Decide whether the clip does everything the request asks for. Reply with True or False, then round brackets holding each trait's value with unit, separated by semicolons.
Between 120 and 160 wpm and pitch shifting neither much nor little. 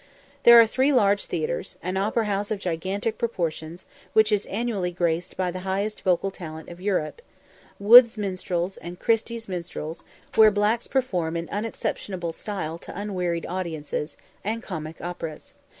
True (150 wpm; 4.0 semitones)